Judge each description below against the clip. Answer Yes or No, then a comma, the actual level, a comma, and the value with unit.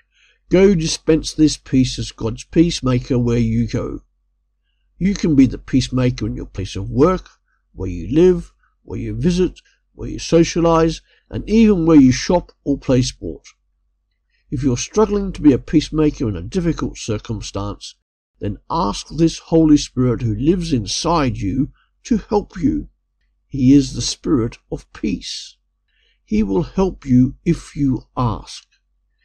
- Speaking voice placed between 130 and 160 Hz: Yes, medium, 140 Hz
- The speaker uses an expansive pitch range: Yes, wide, 5.8 semitones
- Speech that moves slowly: No, average, 150 wpm